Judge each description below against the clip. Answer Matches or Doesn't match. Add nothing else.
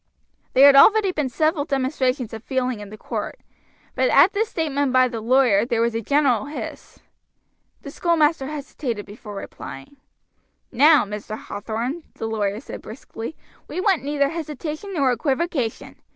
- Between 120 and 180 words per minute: Matches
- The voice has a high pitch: Matches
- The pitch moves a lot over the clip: Doesn't match